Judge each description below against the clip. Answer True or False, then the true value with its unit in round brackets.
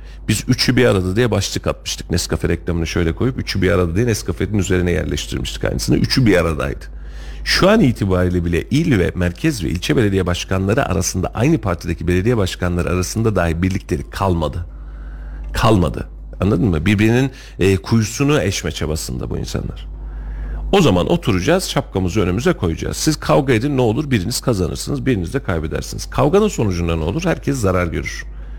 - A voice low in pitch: True (95 Hz)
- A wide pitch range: True (5.9 semitones)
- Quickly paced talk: True (155 wpm)